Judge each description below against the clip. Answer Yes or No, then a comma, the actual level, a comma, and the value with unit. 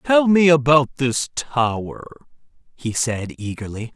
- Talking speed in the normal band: No, slow, 120 wpm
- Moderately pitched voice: No, low, 130 Hz